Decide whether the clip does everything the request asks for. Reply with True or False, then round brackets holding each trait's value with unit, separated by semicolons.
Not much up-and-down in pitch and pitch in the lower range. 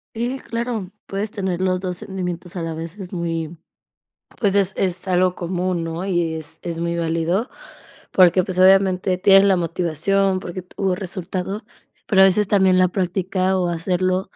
False (1.9 semitones; 185 Hz)